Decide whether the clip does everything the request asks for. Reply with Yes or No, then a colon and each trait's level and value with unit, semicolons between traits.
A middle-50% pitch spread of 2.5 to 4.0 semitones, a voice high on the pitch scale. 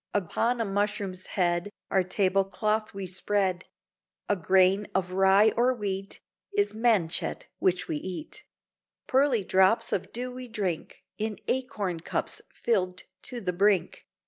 Yes: average, 3.2 semitones; high, 195 Hz